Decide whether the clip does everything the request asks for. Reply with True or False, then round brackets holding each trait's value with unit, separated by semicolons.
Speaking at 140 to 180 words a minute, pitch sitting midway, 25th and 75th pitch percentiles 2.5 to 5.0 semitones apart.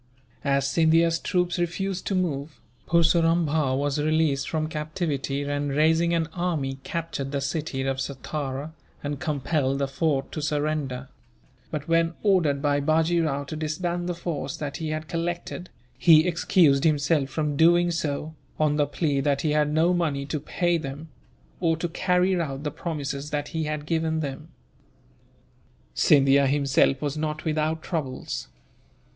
True (155 wpm; 155 Hz; 2.8 semitones)